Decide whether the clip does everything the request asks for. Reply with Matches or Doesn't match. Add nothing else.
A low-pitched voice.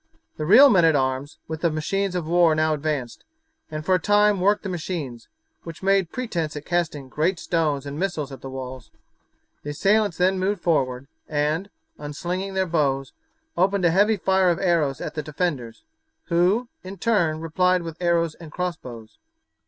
Doesn't match